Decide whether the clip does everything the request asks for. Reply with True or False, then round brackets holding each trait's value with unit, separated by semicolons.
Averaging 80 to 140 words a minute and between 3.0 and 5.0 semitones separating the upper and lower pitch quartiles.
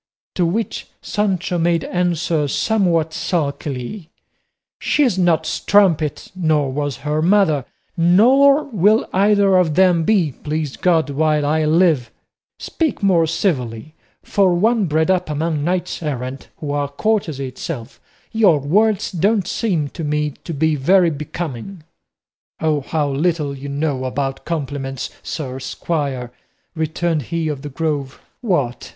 True (135 wpm; 4.2 semitones)